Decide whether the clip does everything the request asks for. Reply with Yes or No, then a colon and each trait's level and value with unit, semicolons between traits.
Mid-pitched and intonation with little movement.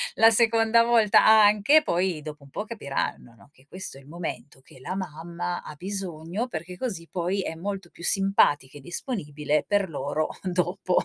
No: medium, 180 Hz; average, 4.8 semitones